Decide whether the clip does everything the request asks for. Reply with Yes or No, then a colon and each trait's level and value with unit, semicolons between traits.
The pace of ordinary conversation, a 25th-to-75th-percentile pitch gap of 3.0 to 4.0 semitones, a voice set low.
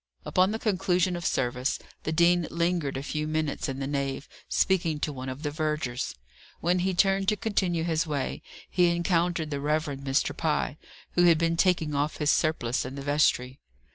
No: average, 185 wpm; average, 3.7 semitones; medium, 155 Hz